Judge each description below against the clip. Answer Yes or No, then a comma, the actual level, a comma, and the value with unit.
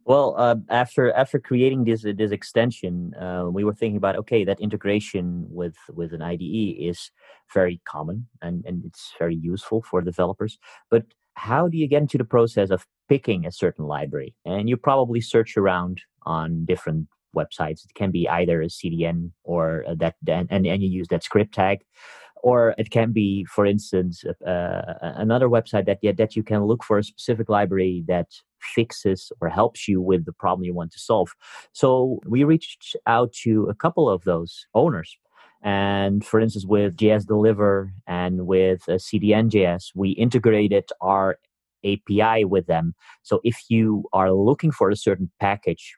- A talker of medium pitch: No, low, 100 Hz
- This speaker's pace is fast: No, average, 170 wpm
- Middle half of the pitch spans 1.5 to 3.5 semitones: No, average, 3.9 semitones